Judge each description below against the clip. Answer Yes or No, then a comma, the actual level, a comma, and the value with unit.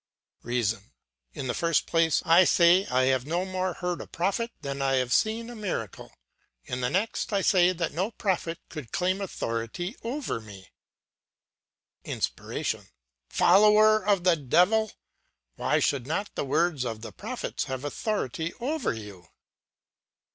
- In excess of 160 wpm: No, average, 145 wpm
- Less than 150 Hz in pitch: No, medium, 170 Hz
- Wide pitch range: Yes, wide, 7.4 semitones